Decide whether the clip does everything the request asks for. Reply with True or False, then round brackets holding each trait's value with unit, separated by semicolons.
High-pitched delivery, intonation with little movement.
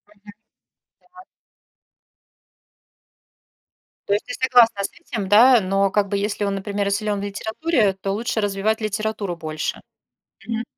True (205 Hz; 2.0 semitones)